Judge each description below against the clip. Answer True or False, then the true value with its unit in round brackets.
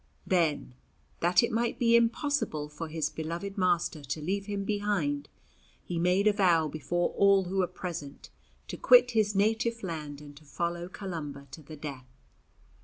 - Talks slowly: False (165 wpm)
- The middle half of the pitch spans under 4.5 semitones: False (4.9 semitones)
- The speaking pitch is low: False (175 Hz)